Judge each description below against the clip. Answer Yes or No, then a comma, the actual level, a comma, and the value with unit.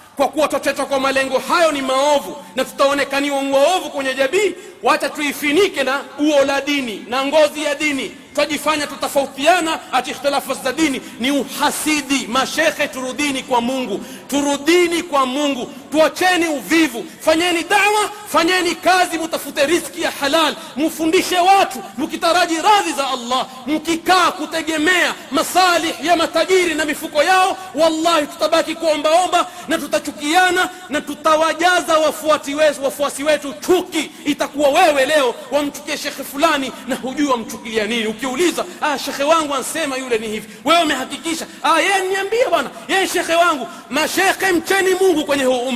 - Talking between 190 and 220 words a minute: No, average, 135 wpm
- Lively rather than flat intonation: No, average, 3.4 semitones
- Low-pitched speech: No, very high, 300 Hz